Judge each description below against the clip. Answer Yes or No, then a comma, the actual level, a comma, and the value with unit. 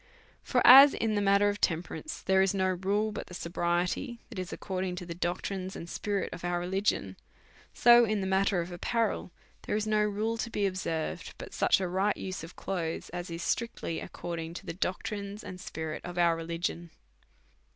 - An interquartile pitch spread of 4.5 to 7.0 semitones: No, average, 3.0 semitones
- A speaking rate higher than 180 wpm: Yes, average, 195 wpm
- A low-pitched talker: No, medium, 185 Hz